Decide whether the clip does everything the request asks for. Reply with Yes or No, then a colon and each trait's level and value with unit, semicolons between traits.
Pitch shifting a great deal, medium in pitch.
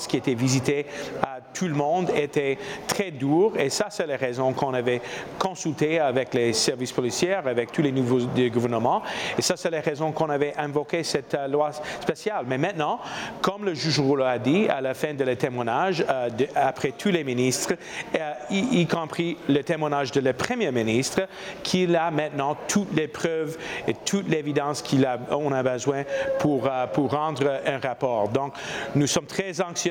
No: average, 3.9 semitones; medium, 145 Hz